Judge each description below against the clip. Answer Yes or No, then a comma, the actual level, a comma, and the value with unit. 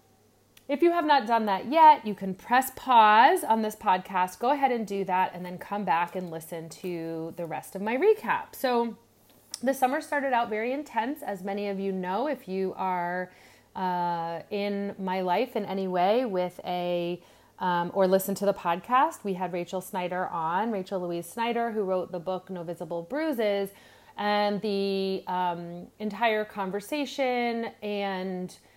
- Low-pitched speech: No, high, 195 Hz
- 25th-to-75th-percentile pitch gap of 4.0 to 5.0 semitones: Yes, average, 4.4 semitones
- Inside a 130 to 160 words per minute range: No, average, 170 wpm